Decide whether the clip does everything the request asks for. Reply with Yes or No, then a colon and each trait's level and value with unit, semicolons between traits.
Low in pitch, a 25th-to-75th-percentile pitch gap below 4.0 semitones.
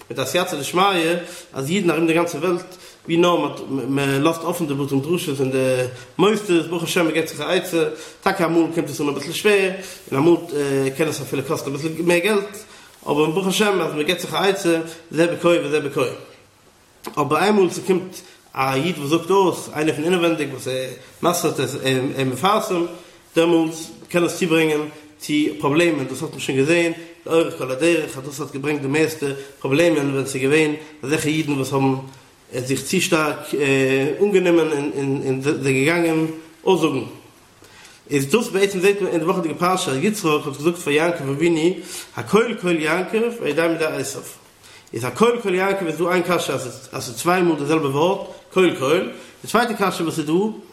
No: medium, 165 Hz; average, 3.6 semitones